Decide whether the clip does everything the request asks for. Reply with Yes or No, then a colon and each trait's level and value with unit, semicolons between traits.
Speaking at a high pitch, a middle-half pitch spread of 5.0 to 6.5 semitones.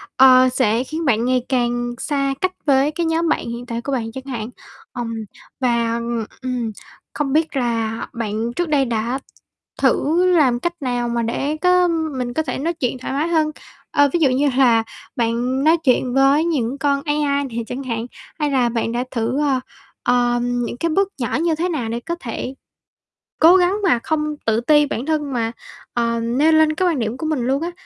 No: very high, 260 Hz; average, 4.3 semitones